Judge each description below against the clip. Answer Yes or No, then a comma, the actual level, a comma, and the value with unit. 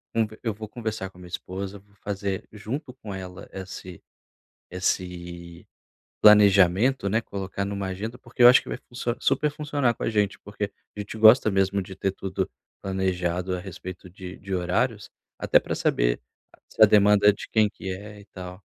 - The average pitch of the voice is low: Yes, low, 100 Hz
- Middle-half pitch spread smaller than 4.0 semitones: Yes, average, 2.7 semitones